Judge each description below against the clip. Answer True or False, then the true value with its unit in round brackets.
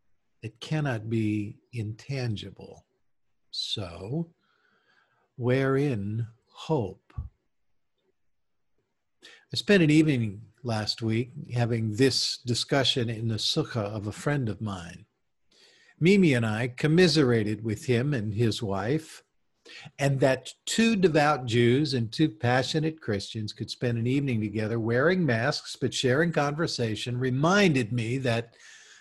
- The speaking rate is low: True (115 wpm)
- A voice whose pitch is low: True (125 Hz)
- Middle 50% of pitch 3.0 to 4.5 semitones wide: False (5.0 semitones)